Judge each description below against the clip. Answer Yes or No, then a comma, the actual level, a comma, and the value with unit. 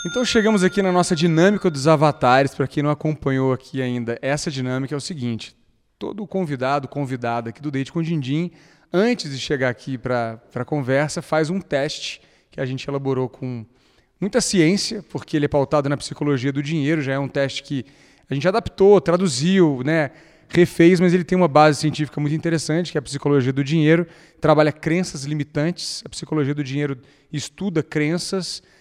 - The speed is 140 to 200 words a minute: Yes, average, 180 wpm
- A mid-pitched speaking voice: Yes, medium, 150 Hz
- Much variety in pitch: No, average, 3.6 semitones